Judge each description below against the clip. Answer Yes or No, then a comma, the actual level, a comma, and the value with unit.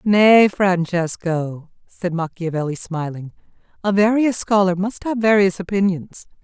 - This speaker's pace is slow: Yes, slow, 110 wpm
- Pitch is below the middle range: No, medium, 185 Hz